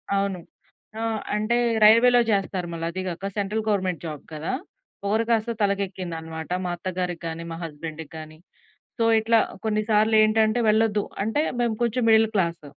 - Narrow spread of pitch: No, average, 4.3 semitones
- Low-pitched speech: No, high, 200 Hz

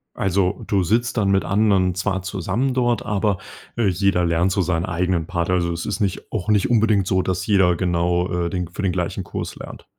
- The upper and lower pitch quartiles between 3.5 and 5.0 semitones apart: No, narrow, 2.5 semitones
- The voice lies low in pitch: Yes, very low, 95 Hz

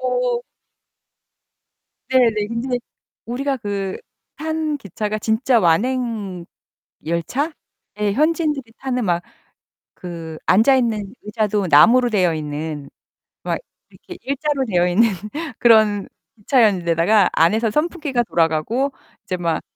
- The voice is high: Yes, high, 220 Hz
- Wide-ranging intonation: Yes, wide, 5.9 semitones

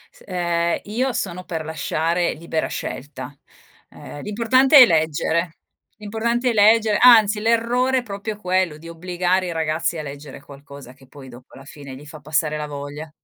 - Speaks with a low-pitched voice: No, medium, 170 Hz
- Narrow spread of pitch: No, wide, 6.0 semitones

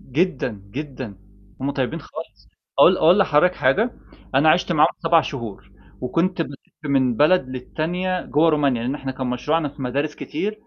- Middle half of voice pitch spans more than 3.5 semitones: Yes, average, 4.3 semitones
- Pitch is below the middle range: No, medium, 150 Hz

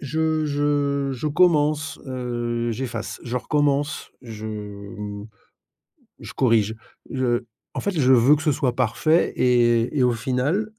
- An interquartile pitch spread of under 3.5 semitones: No, average, 3.8 semitones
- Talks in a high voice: No, low, 130 Hz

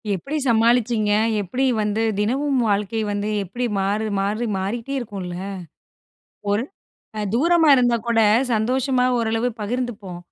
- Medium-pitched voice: No, high, 225 Hz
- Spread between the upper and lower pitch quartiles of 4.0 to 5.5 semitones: No, average, 3.3 semitones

